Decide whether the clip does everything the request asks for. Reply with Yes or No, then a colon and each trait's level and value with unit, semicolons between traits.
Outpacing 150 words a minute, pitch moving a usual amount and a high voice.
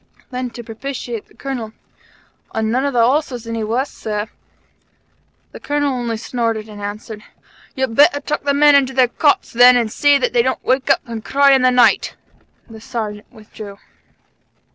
Yes: average, 180 wpm; average, 3.5 semitones; high, 245 Hz